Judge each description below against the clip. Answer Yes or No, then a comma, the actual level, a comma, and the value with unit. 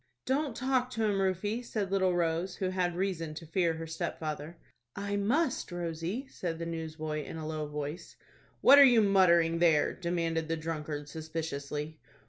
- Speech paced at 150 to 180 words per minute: Yes, average, 165 wpm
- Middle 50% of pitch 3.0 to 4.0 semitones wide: Yes, average, 3.7 semitones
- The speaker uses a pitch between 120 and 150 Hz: No, medium, 170 Hz